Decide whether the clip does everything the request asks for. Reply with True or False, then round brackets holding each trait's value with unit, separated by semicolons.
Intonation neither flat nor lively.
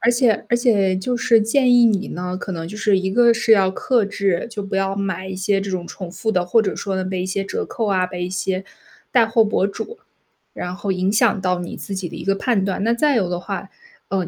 True (3.2 semitones)